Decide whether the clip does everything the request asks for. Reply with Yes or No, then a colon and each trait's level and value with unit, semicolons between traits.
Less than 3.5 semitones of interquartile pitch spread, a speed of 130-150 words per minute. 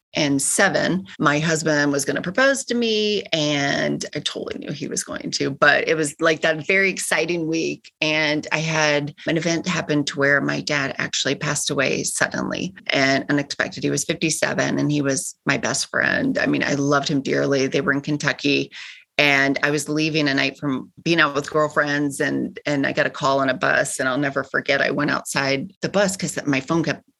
No: narrow, 2.4 semitones; fast, 205 wpm